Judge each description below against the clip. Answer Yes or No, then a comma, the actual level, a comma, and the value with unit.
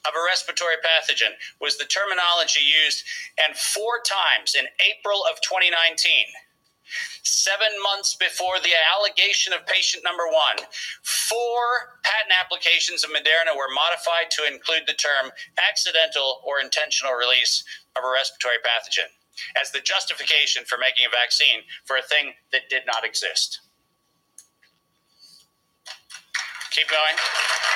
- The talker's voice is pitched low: No, medium, 170 Hz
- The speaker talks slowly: Yes, slow, 130 wpm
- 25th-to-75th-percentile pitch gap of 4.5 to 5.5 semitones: Yes, average, 4.8 semitones